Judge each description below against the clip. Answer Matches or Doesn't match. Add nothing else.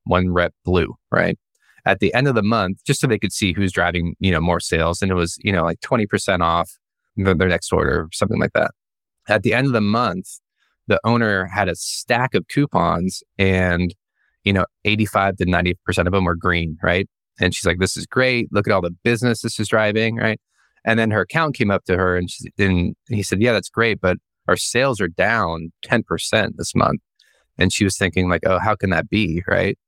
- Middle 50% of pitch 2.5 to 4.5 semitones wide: Matches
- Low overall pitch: Matches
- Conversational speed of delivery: Doesn't match